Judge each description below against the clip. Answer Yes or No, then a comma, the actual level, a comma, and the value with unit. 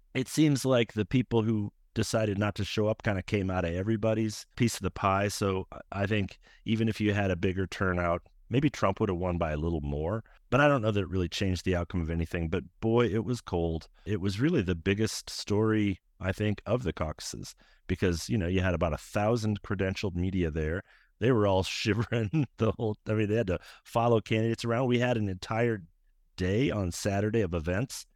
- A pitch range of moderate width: Yes, average, 3.5 semitones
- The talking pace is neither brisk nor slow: No, fast, 215 wpm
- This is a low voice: Yes, low, 105 Hz